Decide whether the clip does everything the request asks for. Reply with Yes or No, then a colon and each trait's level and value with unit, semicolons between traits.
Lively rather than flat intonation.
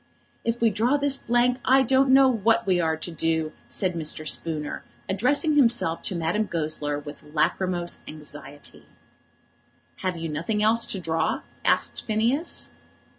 Yes: wide, 6.9 semitones